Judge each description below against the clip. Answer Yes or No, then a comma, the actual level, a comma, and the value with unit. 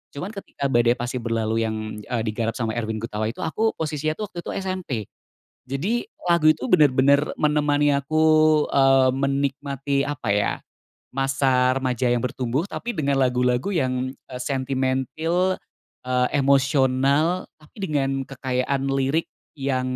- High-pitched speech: No, low, 135 Hz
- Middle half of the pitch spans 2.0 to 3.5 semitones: Yes, average, 2.9 semitones